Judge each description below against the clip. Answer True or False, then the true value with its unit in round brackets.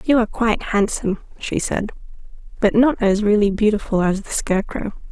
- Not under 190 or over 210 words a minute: False (165 wpm)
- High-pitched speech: True (210 Hz)